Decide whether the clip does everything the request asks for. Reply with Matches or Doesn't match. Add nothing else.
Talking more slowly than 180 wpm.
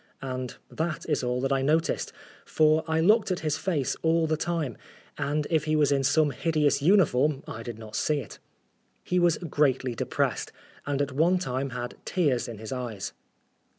Doesn't match